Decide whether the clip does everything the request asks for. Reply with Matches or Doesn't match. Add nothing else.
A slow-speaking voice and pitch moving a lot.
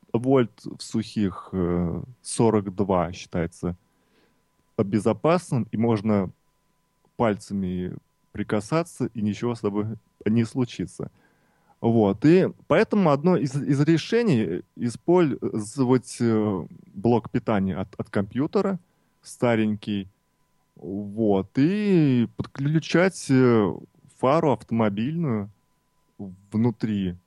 Matches